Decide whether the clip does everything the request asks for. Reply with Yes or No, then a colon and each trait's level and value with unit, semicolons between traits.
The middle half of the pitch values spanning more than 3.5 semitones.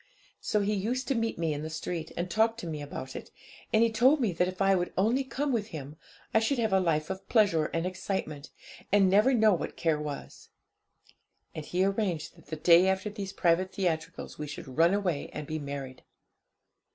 Yes: average, 5.1 semitones